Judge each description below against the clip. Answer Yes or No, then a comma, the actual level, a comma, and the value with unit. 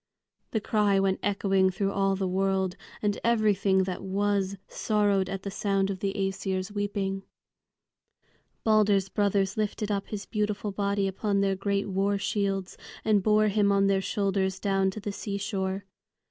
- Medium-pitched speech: No, high, 200 Hz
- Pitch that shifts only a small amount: Yes, narrow, 1.1 semitones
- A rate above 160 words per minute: No, average, 155 wpm